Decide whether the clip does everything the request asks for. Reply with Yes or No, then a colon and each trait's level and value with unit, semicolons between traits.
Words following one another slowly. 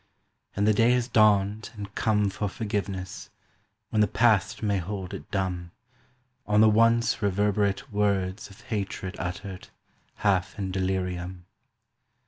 Yes: slow, 130 wpm